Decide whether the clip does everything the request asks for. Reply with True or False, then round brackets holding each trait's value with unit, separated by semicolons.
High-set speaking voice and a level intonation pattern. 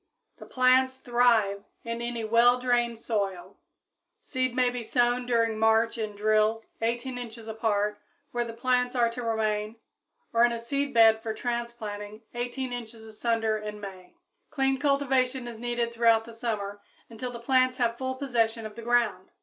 True (235 Hz; 2.0 semitones)